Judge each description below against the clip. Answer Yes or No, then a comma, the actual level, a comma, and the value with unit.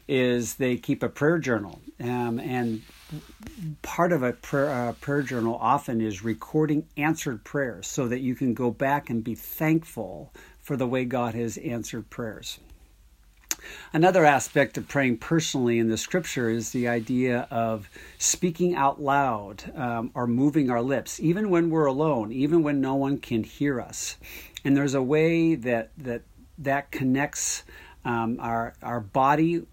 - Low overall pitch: Yes, low, 130 Hz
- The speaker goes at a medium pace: Yes, average, 160 wpm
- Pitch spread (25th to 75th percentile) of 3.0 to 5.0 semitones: Yes, average, 3.8 semitones